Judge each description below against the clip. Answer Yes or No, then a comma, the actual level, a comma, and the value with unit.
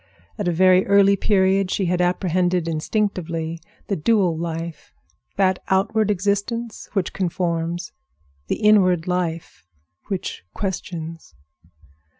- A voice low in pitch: No, medium, 185 Hz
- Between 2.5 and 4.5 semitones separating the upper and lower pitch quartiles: Yes, average, 2.9 semitones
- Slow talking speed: Yes, slow, 105 wpm